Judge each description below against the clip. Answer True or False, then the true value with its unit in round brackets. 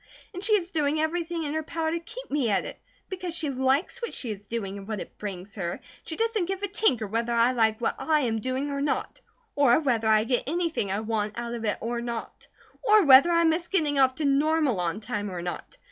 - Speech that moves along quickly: True (240 wpm)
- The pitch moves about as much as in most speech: False (6.7 semitones)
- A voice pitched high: True (270 Hz)